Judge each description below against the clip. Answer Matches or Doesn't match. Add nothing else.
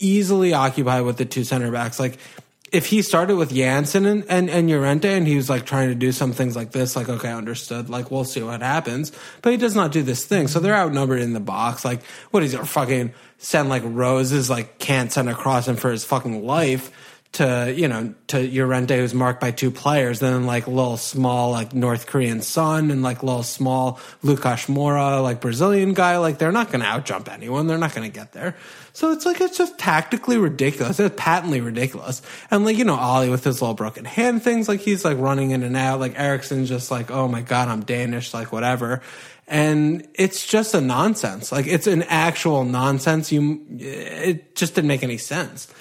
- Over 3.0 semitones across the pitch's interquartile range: Matches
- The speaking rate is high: Matches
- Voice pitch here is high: Doesn't match